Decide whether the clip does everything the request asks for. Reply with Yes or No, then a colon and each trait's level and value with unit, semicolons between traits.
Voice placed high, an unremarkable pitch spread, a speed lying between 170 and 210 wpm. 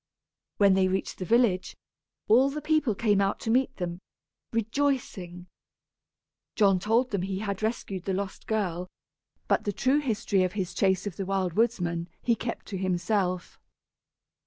No: high, 200 Hz; average, 3.7 semitones; average, 160 wpm